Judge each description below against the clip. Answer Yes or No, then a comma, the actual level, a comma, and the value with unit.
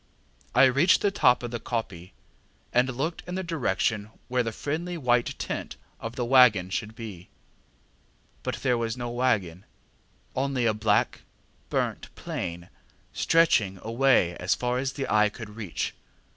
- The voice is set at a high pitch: No, low, 120 Hz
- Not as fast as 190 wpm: Yes, average, 150 wpm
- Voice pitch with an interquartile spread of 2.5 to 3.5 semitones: No, average, 3.9 semitones